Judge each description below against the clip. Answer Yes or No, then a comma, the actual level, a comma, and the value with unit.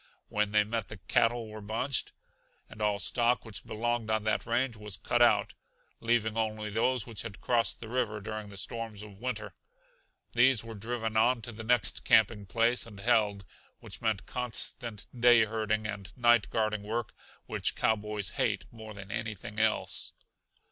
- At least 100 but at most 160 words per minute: No, average, 170 wpm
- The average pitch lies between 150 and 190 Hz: No, low, 110 Hz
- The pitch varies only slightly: Yes, narrow, 1.9 semitones